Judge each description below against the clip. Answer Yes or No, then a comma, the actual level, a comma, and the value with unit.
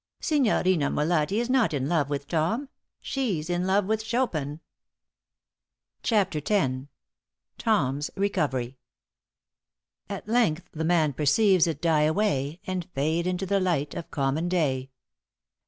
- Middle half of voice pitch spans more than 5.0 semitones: Yes, wide, 5.5 semitones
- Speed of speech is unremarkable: No, slow, 125 wpm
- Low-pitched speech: No, medium, 170 Hz